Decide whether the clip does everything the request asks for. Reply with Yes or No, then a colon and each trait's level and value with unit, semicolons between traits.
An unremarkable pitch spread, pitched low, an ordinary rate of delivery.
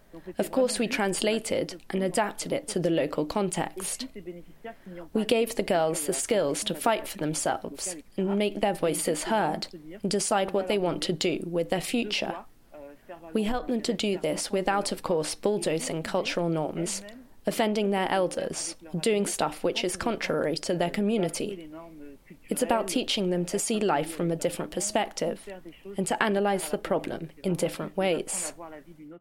No: average, 3.7 semitones; high, 190 Hz; average, 160 wpm